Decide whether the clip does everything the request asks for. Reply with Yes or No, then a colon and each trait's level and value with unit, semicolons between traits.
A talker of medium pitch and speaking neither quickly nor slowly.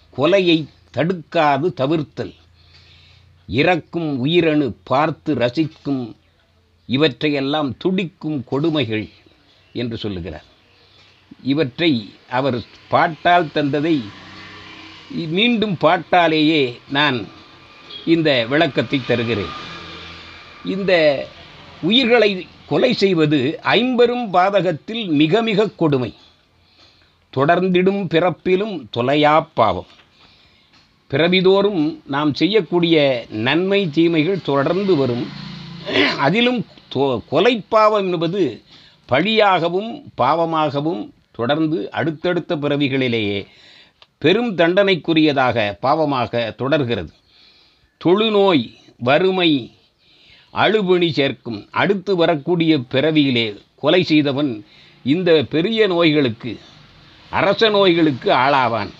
No: medium, 155 Hz; slow, 70 wpm